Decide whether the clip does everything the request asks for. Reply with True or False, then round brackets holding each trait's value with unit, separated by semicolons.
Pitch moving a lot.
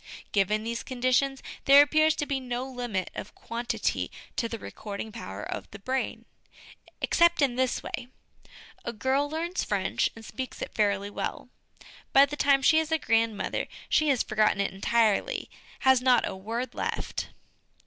False (3.9 semitones)